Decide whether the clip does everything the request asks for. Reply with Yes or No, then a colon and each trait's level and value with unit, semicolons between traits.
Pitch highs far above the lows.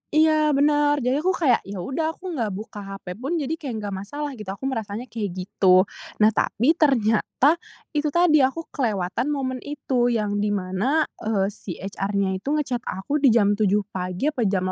Yes: wide, 6.5 semitones